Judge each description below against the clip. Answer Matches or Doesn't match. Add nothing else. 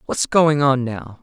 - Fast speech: Doesn't match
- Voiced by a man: Matches